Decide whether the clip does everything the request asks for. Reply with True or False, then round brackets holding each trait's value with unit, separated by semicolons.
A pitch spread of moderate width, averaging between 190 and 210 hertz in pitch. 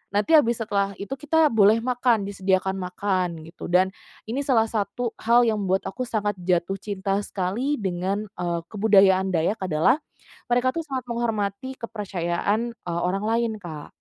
True (3.8 semitones; 205 Hz)